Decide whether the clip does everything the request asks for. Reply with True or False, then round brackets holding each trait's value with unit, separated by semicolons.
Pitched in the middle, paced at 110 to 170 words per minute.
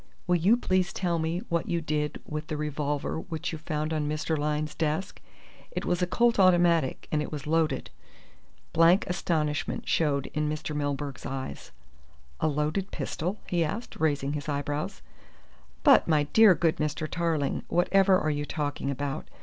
True (155 Hz; 165 wpm)